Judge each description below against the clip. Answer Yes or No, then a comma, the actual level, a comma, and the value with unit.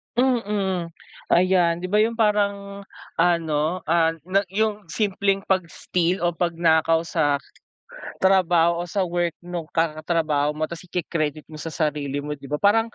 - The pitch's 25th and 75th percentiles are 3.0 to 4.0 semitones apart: Yes, average, 3.4 semitones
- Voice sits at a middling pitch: Yes, medium, 175 Hz